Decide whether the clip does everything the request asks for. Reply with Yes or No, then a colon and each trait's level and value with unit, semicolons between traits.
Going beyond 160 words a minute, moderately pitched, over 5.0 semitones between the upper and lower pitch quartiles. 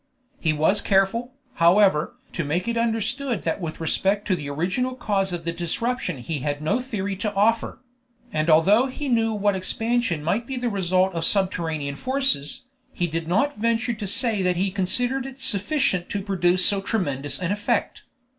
No: average, 175 wpm; high, 195 Hz; wide, 5.4 semitones